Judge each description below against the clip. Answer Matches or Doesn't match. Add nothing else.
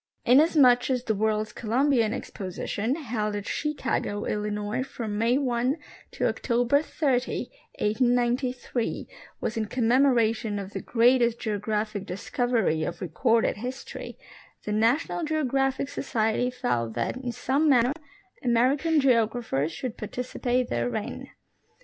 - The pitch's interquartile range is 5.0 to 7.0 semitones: Doesn't match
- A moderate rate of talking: Doesn't match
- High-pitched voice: Matches